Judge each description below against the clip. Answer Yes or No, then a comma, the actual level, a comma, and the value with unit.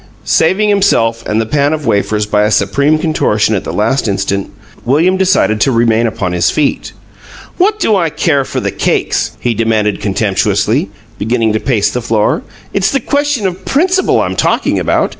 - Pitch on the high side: No, low, 120 Hz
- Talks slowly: No, average, 180 wpm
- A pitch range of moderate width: No, wide, 8.8 semitones